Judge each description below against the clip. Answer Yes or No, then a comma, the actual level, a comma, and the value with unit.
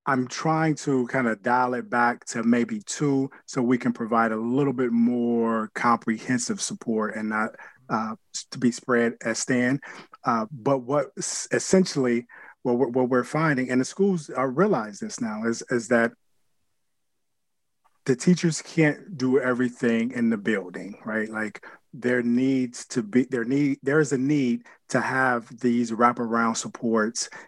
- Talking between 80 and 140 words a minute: No, average, 155 wpm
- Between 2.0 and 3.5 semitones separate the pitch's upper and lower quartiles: Yes, average, 2.9 semitones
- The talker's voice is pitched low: Yes, low, 125 Hz